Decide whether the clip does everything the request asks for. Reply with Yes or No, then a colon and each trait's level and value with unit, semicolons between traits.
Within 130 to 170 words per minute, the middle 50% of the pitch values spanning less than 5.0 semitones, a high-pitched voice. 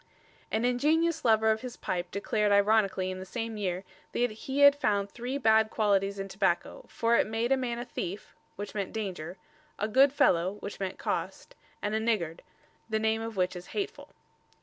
No: average, 195 wpm; average, 3.5 semitones; high, 220 Hz